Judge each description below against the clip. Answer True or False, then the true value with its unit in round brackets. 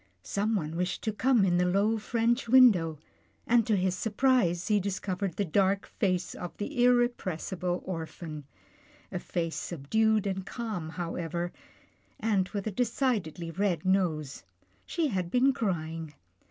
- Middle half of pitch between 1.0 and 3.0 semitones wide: False (4.4 semitones)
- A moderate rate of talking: True (145 wpm)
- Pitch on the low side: False (190 Hz)